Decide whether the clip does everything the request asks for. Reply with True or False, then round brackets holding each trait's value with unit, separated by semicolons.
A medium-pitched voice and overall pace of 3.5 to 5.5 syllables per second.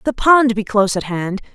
False (220 Hz; 5.3 syllables/s)